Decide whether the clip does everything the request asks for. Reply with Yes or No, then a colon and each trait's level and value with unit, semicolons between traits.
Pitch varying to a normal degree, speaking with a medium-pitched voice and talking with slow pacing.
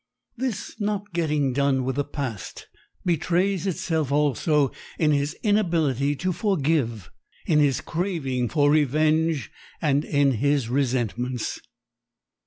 Yes: average, 3.9 semitones; medium, 145 Hz; slow, 115 wpm